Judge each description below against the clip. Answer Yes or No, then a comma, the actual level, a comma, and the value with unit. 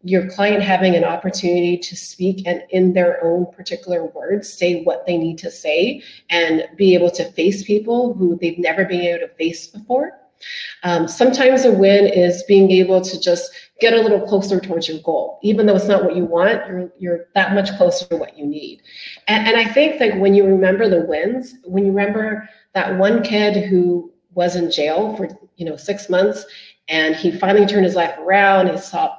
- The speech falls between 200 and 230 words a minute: Yes, fast, 205 wpm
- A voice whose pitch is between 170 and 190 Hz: Yes, medium, 185 Hz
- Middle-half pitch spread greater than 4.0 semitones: No, average, 2.8 semitones